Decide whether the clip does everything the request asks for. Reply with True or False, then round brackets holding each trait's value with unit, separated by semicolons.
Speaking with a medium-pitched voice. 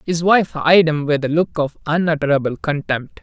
True (155 Hz)